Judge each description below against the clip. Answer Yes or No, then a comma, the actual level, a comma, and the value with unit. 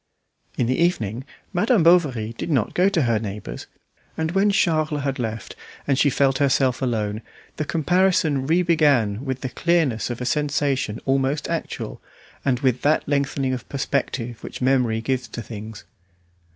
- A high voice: No, low, 135 Hz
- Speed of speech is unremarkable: Yes, average, 160 wpm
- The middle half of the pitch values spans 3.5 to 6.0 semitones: Yes, average, 4.5 semitones